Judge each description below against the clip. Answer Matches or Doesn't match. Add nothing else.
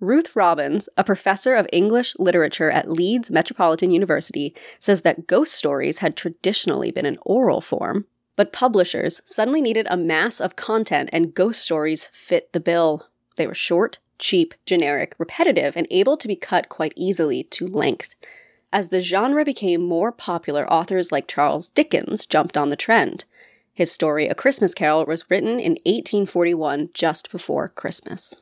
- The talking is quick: Doesn't match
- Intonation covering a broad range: Matches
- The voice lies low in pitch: Doesn't match